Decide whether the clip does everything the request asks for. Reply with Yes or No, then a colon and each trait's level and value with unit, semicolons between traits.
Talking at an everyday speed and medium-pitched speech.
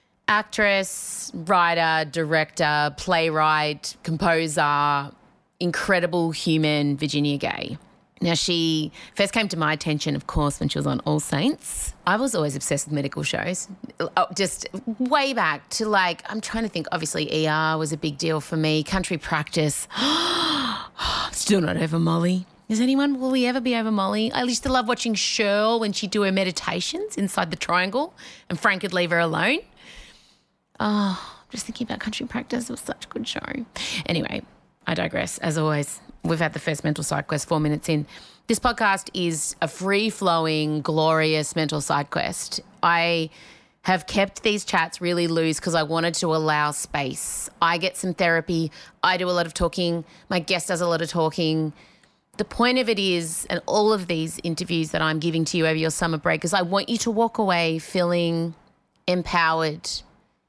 Yes: average, 175 wpm; medium, 170 Hz